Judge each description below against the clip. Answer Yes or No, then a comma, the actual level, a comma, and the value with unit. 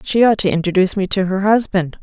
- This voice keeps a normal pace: No, fast, 235 wpm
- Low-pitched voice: No, high, 195 Hz